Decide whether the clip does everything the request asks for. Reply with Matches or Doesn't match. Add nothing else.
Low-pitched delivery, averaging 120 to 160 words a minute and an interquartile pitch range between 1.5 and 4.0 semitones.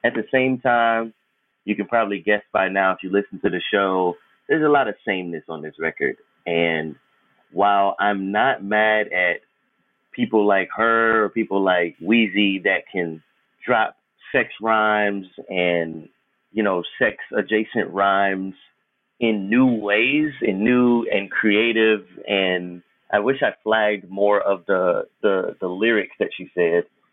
Matches